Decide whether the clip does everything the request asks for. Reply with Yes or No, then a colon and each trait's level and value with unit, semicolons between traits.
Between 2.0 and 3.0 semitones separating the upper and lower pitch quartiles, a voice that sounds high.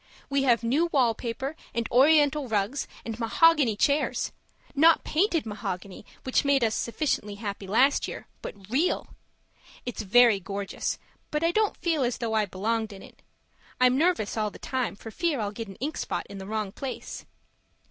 No: average, 5.2 semitones; high, 240 Hz